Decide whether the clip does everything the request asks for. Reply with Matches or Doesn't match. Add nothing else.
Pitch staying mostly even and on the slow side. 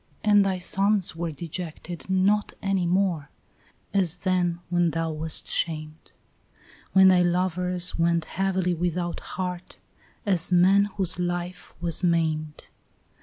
Matches